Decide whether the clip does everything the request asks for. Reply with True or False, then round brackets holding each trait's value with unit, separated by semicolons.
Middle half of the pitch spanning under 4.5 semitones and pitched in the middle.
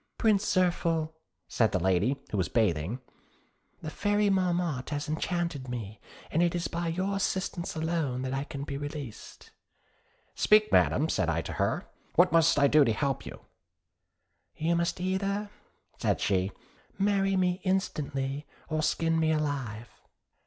False (5.4 semitones; 155 Hz)